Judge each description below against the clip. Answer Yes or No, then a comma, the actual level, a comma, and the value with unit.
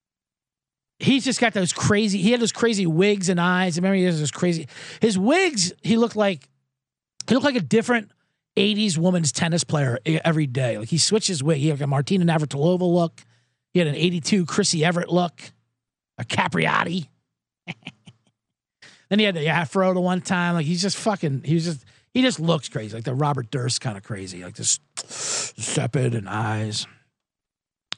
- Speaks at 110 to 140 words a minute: No, average, 180 wpm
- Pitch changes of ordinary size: No, wide, 5.9 semitones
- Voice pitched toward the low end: No, medium, 170 Hz